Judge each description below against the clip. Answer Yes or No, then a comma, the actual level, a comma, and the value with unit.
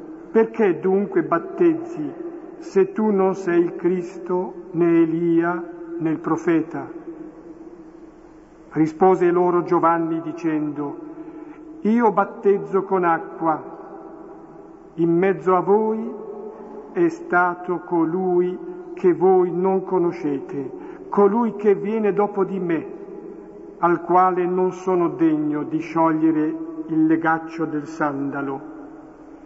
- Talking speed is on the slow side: Yes, slow, 100 wpm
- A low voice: No, high, 190 Hz